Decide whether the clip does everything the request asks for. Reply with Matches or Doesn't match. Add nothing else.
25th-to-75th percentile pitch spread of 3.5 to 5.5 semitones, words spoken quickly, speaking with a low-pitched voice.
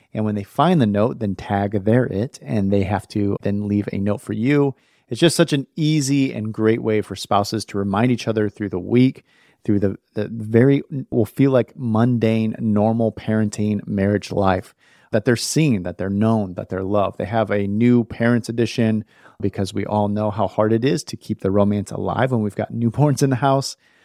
Doesn't match